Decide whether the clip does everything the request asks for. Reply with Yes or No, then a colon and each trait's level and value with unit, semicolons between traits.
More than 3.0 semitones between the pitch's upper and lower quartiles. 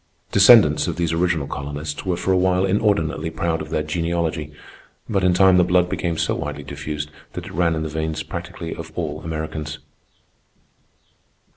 No: narrow, 2.6 semitones